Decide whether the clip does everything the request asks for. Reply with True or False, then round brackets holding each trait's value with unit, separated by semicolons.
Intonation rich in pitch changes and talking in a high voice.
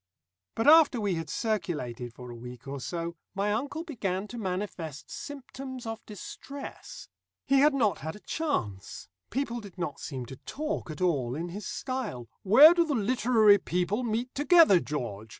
True (8.6 semitones; 205 Hz)